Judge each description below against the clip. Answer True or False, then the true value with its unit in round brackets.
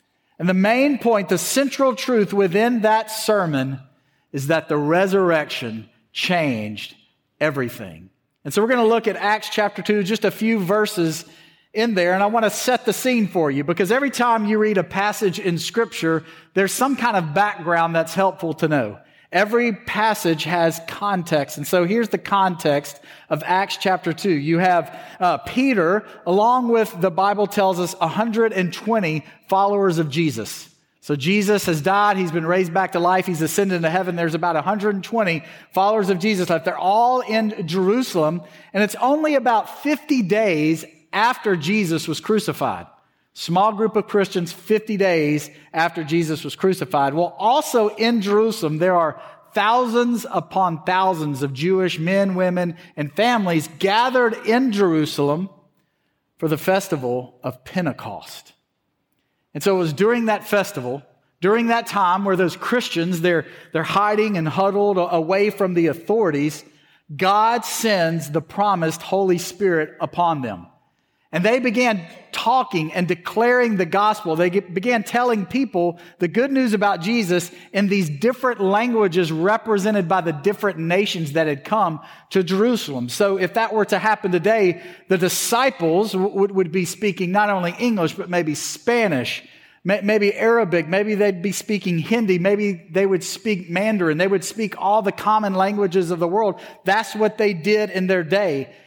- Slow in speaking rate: False (160 wpm)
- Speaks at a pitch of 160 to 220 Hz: True (190 Hz)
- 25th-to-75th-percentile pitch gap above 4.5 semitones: False (4.2 semitones)